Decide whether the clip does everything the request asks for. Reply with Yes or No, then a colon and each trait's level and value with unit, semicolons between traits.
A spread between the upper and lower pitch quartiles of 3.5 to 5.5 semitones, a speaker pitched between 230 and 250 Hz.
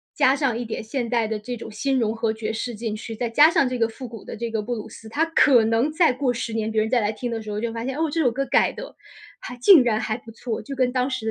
No: average, 2.9 semitones; high, 235 Hz